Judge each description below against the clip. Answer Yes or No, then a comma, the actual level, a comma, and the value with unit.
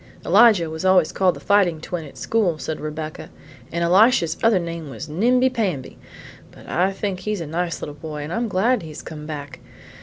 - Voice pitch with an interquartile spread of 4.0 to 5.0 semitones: Yes, average, 4.5 semitones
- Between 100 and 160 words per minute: No, average, 195 wpm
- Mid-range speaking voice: Yes, medium, 170 Hz